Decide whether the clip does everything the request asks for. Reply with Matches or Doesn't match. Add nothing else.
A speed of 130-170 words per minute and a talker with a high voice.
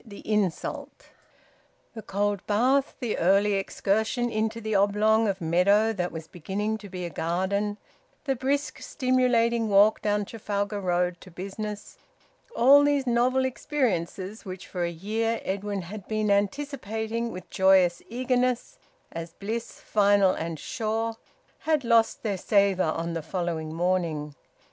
Matches